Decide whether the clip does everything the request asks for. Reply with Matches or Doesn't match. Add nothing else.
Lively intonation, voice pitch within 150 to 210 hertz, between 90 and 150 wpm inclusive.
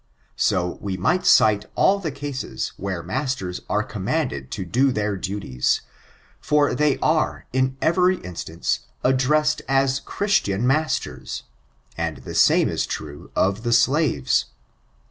Doesn't match